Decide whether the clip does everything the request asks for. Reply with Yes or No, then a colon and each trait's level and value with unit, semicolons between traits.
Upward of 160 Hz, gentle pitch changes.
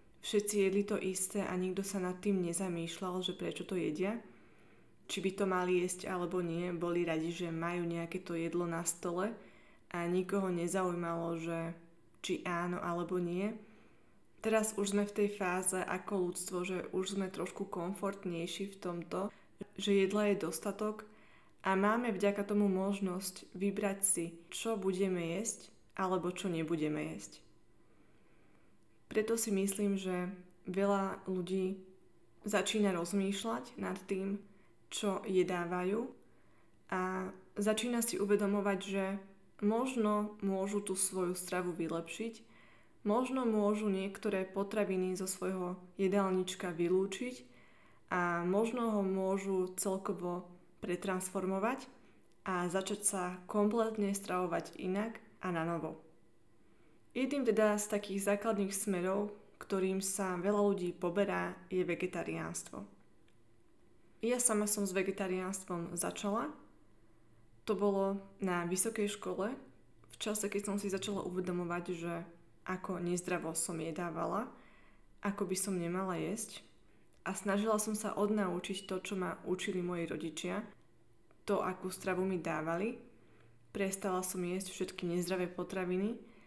Yes: high, 190 Hz; narrow, 2.3 semitones